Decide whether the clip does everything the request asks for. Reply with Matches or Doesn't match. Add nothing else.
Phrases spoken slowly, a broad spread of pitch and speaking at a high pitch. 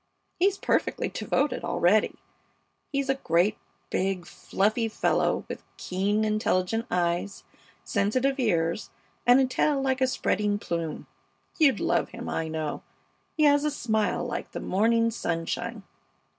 Matches